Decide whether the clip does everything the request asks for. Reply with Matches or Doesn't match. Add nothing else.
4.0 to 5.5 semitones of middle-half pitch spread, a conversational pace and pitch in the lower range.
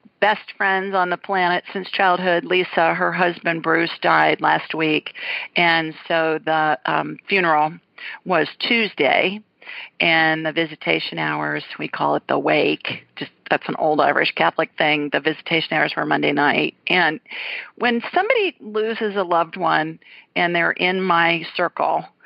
Doesn't match